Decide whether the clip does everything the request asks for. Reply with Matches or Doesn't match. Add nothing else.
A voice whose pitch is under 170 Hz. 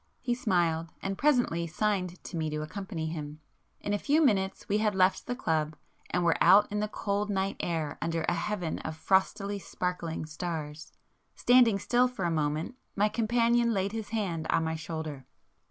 Doesn't match